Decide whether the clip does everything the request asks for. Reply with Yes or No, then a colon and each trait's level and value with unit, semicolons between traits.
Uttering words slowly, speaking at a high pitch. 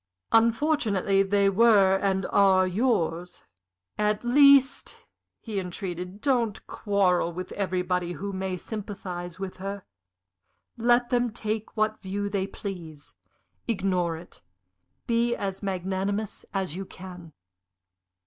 Yes: slow, 110 wpm; high, 195 Hz